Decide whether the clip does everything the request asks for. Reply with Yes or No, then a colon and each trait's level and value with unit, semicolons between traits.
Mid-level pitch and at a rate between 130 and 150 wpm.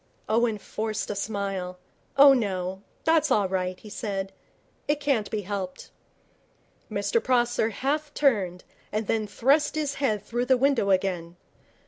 No: high, 215 Hz; slow, 135 wpm